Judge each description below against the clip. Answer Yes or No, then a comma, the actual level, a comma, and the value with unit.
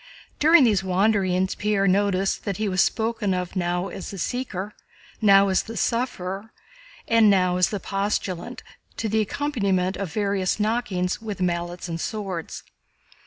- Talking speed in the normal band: Yes, average, 150 wpm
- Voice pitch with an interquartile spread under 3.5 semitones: Yes, average, 2.9 semitones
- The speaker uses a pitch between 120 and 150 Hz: No, high, 195 Hz